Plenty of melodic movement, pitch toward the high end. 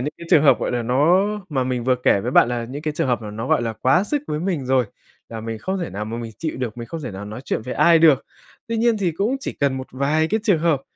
No: wide, 5.8 semitones; low, 135 Hz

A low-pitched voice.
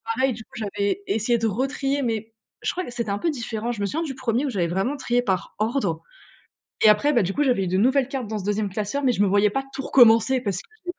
No: high, 225 Hz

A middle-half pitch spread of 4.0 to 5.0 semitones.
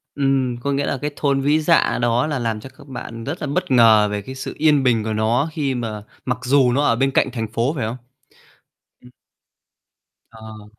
No: average, 3.6 semitones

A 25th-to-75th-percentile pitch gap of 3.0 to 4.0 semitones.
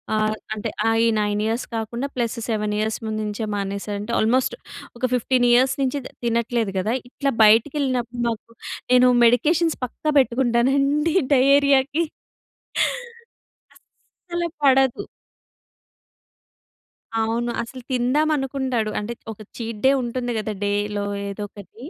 Yes: average, 3.6 semitones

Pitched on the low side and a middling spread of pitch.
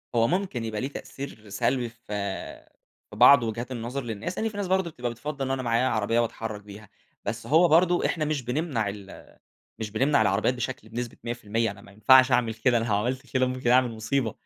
Yes: low, 120 Hz; average, 3.4 semitones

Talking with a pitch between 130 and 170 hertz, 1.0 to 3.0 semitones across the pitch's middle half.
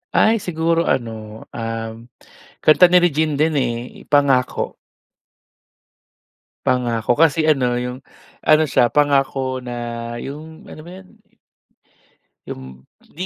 No: low, 135 Hz; average, 4.8 semitones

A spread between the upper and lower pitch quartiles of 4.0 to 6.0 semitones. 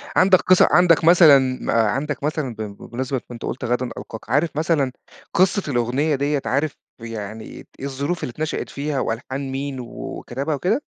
Yes: average, 4.3 semitones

